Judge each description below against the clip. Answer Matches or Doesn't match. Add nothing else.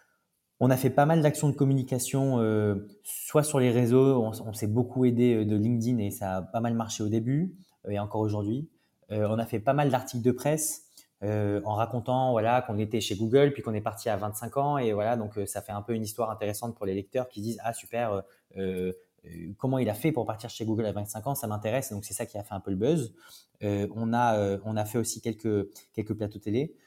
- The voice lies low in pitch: Matches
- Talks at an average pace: Doesn't match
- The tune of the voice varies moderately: Matches